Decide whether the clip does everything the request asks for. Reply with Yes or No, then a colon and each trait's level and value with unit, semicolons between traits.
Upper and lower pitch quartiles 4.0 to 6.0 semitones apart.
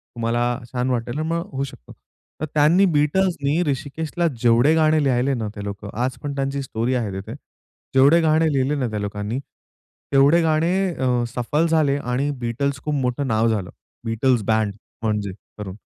Yes: average, 4.6 semitones